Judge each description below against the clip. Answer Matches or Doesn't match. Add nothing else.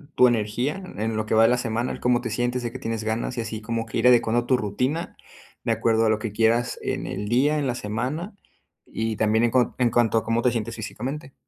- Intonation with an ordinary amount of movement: Doesn't match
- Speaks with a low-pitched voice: Matches